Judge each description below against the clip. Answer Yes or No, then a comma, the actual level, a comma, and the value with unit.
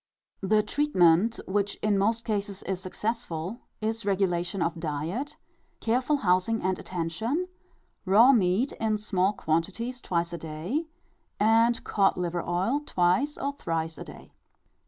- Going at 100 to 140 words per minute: Yes, slow, 135 wpm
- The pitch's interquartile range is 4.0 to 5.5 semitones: Yes, average, 4.7 semitones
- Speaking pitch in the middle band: No, high, 200 Hz